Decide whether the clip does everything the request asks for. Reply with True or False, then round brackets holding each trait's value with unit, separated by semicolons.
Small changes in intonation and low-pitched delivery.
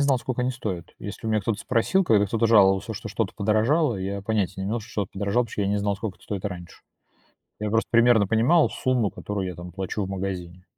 False (3.0 semitones; 105 Hz)